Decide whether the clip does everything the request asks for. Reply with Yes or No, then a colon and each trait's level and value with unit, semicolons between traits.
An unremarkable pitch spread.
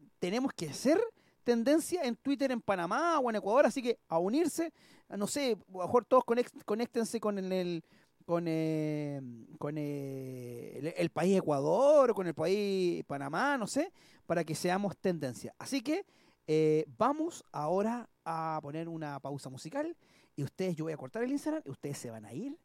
No: wide, 8.7 semitones